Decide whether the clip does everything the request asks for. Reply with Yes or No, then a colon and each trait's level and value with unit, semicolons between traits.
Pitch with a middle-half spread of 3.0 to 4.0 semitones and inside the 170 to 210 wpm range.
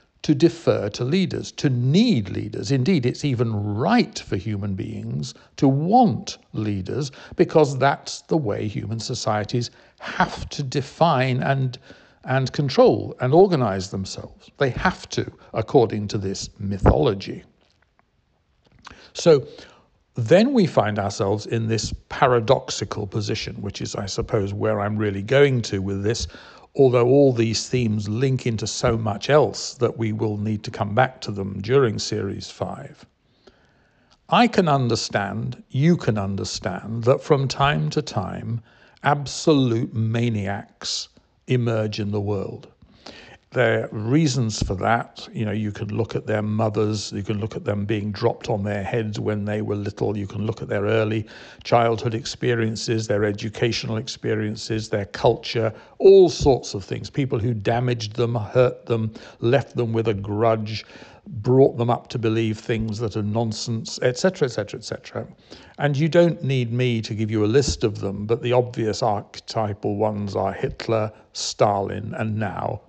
No: average, 3.3 semitones; average, 150 wpm